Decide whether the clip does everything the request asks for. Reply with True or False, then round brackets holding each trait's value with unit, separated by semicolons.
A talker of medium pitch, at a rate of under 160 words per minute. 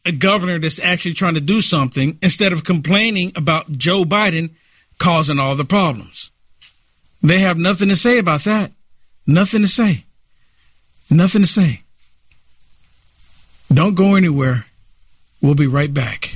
True (160 Hz; 140 wpm)